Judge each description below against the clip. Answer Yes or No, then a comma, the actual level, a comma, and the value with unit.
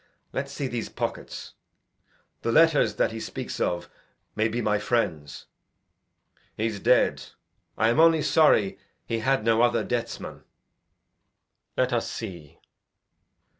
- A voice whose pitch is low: Yes, low, 115 Hz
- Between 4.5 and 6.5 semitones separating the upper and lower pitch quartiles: No, average, 3.4 semitones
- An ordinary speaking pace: No, slow, 125 wpm